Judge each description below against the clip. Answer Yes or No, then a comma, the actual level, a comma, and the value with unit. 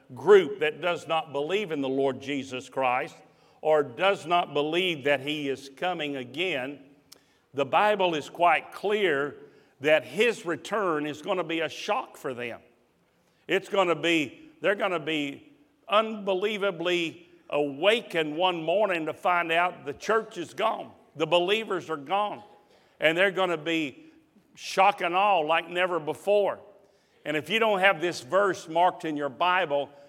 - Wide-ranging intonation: No, average, 4.8 semitones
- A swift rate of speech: No, average, 160 wpm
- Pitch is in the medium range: Yes, medium, 175 Hz